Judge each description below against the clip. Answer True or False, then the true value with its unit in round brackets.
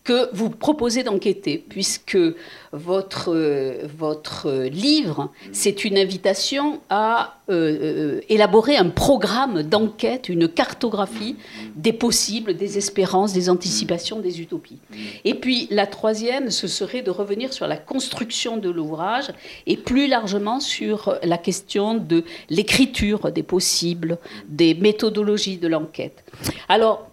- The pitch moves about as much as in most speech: True (4.6 semitones)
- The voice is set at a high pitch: True (205 Hz)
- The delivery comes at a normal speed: False (120 wpm)